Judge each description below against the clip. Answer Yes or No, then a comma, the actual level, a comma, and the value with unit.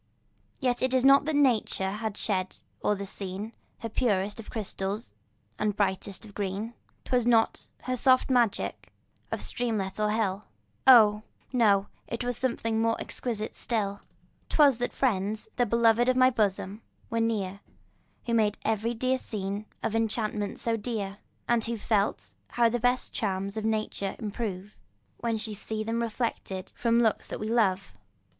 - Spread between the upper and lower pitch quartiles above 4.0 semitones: No, average, 2.7 semitones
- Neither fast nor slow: Yes, average, 155 wpm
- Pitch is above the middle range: Yes, high, 220 Hz